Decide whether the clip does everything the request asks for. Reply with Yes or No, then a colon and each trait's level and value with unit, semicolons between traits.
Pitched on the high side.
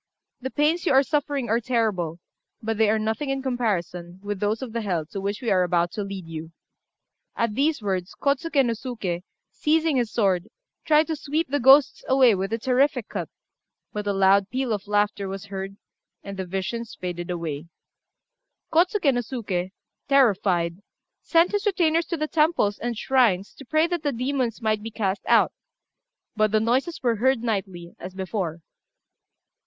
Yes: high, 220 Hz